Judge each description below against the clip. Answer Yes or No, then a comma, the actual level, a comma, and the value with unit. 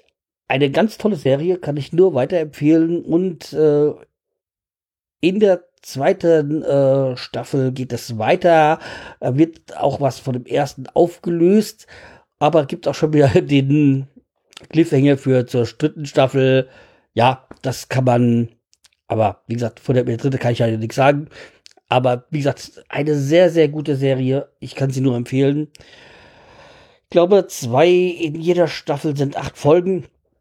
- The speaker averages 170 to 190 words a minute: No, average, 145 wpm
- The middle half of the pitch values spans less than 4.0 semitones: No, average, 4.3 semitones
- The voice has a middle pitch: Yes, medium, 145 Hz